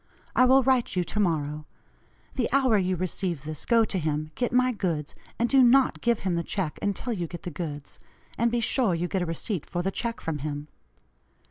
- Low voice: No, medium, 185 Hz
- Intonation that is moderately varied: No, wide, 6.6 semitones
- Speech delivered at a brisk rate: Yes, fast, 215 wpm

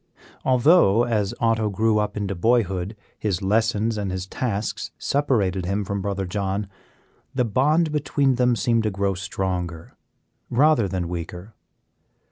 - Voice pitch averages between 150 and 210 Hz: No, low, 105 Hz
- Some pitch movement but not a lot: Yes, average, 3.8 semitones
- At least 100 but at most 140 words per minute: Yes, slow, 135 wpm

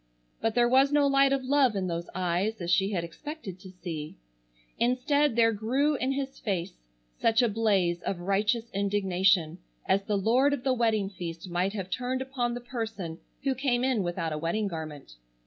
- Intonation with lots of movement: Yes, wide, 5.8 semitones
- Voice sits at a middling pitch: No, high, 215 Hz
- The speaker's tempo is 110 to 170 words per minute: No, average, 185 wpm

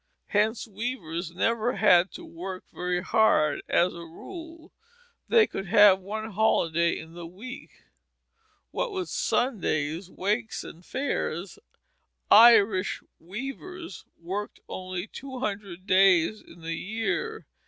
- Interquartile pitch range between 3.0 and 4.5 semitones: No, average, 5.1 semitones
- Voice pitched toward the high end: Yes, high, 200 Hz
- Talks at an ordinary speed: No, slow, 120 wpm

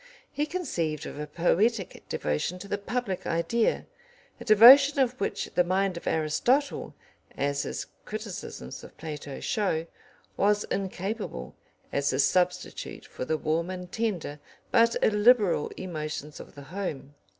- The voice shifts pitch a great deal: Yes, wide, 6.1 semitones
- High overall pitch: No, medium, 180 Hz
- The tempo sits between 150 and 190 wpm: No, average, 140 wpm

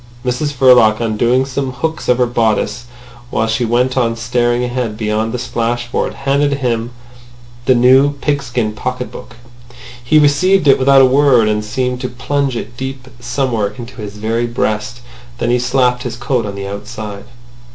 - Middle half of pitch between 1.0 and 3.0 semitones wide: Yes, narrow, 2.5 semitones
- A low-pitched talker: Yes, low, 125 Hz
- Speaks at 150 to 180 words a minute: Yes, average, 170 wpm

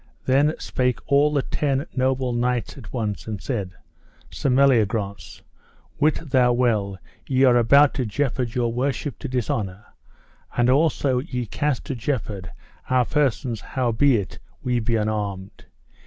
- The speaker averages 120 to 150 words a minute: Yes, average, 140 wpm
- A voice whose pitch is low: Yes, low, 125 Hz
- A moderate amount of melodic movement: Yes, average, 3.5 semitones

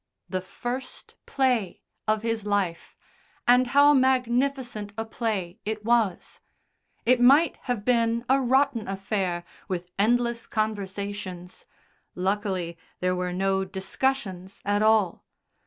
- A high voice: Yes, high, 215 Hz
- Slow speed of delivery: Yes, slow, 115 wpm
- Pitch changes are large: No, average, 4.3 semitones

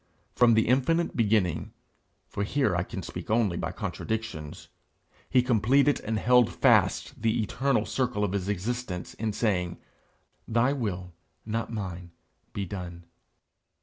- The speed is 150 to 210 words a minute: No, slow, 135 wpm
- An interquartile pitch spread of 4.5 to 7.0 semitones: Yes, average, 4.8 semitones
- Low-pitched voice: Yes, low, 110 Hz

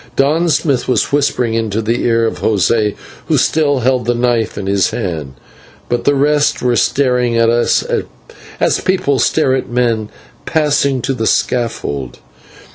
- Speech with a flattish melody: No, average, 3.6 semitones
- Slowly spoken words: No, average, 155 wpm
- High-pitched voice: No, low, 120 Hz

